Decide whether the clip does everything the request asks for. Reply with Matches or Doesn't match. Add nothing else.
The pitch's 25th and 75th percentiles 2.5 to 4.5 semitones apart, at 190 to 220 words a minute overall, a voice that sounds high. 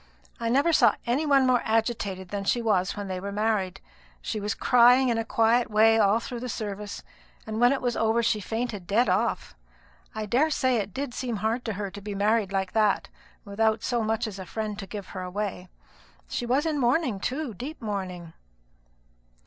Matches